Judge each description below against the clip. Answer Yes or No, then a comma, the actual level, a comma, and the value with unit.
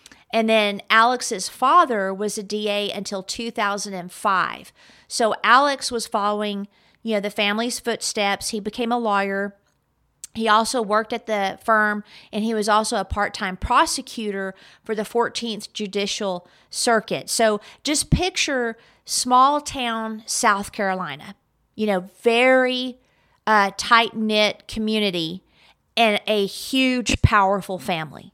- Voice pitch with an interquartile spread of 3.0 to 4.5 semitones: No, narrow, 2.5 semitones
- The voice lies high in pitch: Yes, high, 215 Hz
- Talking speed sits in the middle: No, slow, 125 wpm